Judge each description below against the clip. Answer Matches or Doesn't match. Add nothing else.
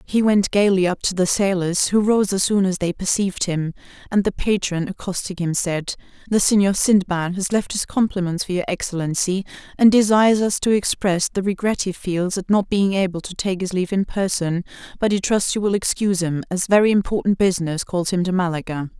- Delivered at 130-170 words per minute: Doesn't match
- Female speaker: Matches